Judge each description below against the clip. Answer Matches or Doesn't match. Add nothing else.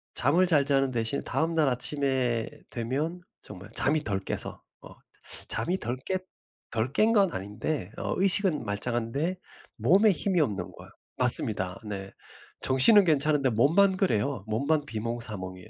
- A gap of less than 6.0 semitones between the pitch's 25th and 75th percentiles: Doesn't match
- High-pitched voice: Doesn't match